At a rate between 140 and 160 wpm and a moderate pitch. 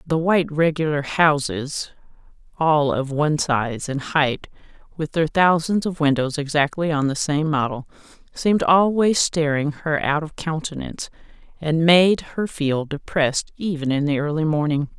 Yes: average, 150 wpm; medium, 155 Hz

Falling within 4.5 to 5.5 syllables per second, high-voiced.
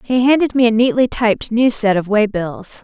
Yes: 5.1 syllables/s; high, 230 Hz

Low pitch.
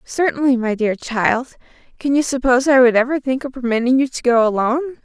No: very high, 255 Hz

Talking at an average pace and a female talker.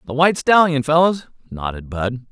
No: average, 155 wpm; male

